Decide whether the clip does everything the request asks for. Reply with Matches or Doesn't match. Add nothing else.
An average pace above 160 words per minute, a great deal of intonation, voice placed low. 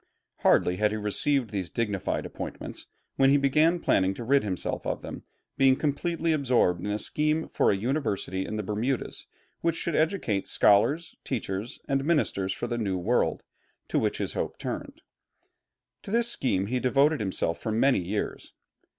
Matches